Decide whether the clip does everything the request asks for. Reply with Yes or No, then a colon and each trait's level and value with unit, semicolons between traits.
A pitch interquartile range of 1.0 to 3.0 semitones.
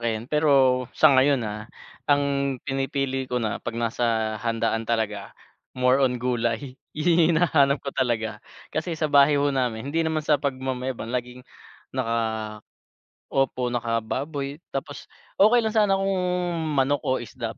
No: average, 3.6 semitones